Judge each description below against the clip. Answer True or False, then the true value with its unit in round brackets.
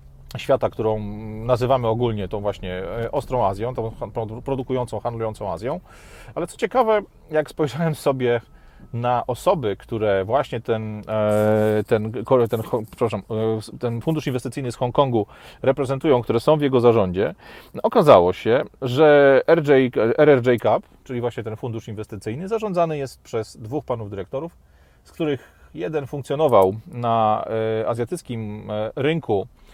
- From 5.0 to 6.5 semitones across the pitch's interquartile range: False (4.0 semitones)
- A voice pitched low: True (120 Hz)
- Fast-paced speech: False (125 wpm)